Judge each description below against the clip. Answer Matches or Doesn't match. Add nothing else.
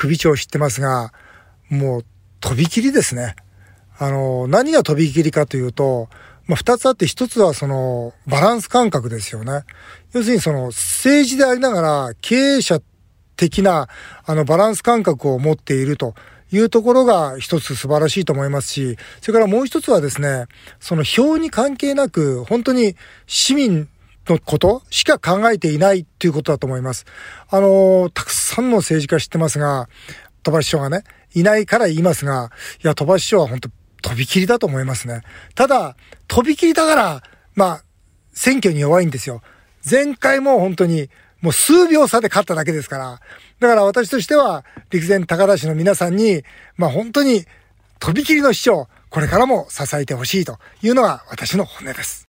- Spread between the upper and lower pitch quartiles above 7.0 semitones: Matches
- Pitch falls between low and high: Matches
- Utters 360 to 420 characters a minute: Doesn't match